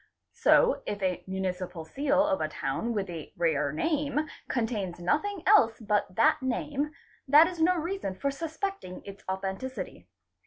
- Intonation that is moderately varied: No, wide, 8.2 semitones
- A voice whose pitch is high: Yes, high, 235 Hz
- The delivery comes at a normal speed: Yes, average, 150 wpm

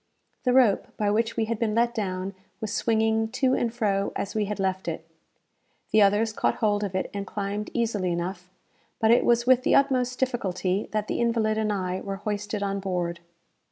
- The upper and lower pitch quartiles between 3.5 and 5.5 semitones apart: No, average, 2.7 semitones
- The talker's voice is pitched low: No, high, 210 Hz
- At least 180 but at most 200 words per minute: Yes, average, 195 wpm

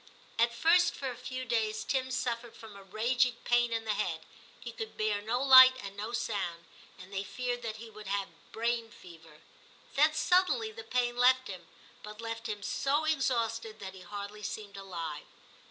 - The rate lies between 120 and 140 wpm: No, average, 185 wpm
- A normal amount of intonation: Yes, average, 3.8 semitones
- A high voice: Yes, high, 225 Hz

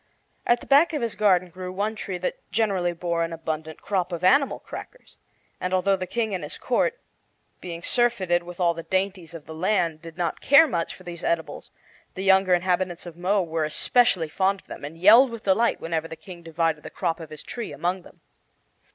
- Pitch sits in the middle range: Yes, medium, 180 Hz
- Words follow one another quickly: Yes, fast, 210 wpm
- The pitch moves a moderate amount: Yes, average, 3.2 semitones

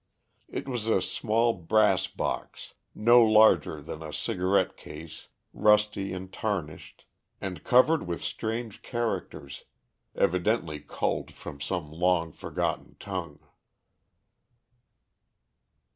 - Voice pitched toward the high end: No, very low, 95 Hz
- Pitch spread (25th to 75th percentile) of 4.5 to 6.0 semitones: Yes, average, 5.0 semitones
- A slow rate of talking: Yes, slow, 100 wpm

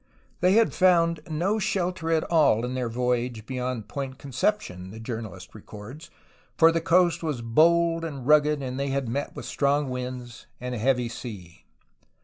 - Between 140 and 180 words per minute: Yes, average, 165 wpm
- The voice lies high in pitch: No, low, 135 Hz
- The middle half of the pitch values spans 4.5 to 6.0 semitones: Yes, wide, 5.4 semitones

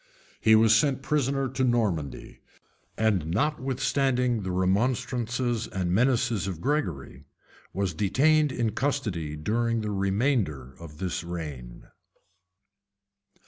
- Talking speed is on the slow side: Yes, slow, 105 wpm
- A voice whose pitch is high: No, low, 110 Hz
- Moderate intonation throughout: No, wide, 6.2 semitones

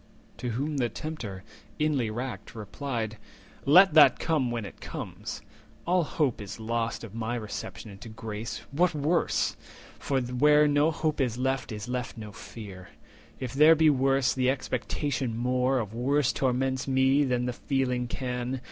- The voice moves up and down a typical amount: Yes, average, 3.6 semitones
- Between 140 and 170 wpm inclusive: Yes, average, 155 wpm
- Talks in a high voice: No, low, 125 Hz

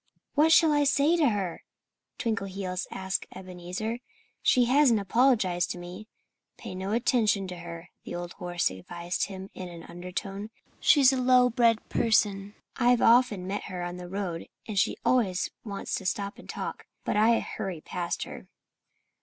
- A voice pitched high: Yes, high, 200 Hz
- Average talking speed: Yes, average, 160 wpm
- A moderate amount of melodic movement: Yes, average, 4.7 semitones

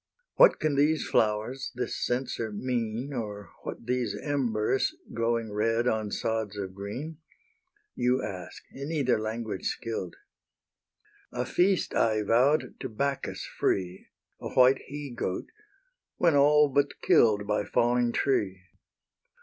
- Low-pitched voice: Yes, low, 120 Hz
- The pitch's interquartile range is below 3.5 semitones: No, average, 4.4 semitones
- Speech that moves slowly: Yes, slow, 125 wpm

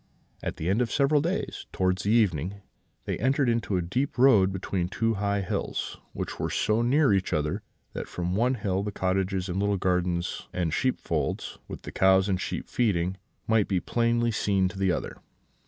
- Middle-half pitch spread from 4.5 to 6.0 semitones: No, average, 4.0 semitones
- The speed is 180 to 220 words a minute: Yes, average, 190 wpm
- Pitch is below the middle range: Yes, low, 100 Hz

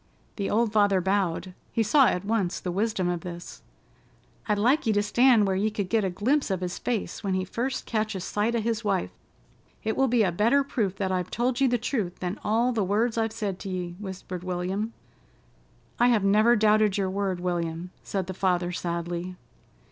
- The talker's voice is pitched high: Yes, high, 205 Hz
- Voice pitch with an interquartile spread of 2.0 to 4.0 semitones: Yes, average, 3.6 semitones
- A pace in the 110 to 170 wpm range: No, average, 200 wpm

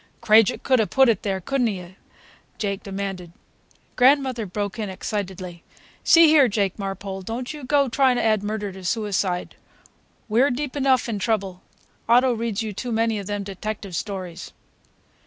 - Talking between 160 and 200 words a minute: Yes, average, 165 wpm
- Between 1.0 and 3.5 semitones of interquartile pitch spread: No, average, 4.1 semitones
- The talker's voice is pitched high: Yes, high, 215 Hz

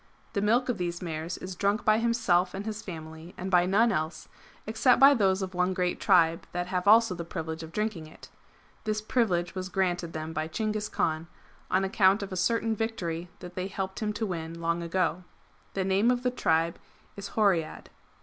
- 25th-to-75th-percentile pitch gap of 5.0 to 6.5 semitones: No, average, 3.9 semitones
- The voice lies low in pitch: No, medium, 185 Hz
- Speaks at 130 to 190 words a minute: No, average, 200 wpm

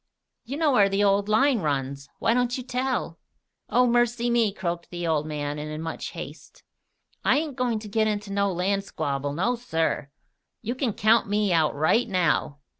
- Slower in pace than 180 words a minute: No, average, 190 wpm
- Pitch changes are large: Yes, wide, 6.9 semitones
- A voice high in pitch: Yes, high, 200 Hz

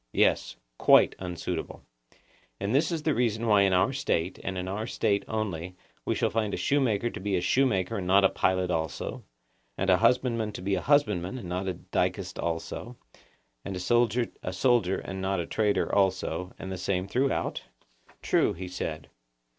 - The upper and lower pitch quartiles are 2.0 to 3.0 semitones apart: No, average, 4.2 semitones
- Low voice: Yes, low, 100 Hz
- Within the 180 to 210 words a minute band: Yes, average, 185 wpm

